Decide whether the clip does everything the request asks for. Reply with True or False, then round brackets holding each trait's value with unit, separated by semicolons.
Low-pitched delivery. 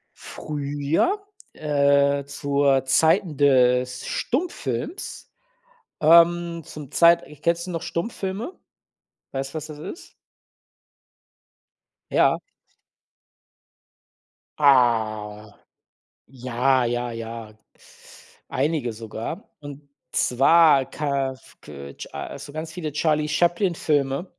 False (145 Hz)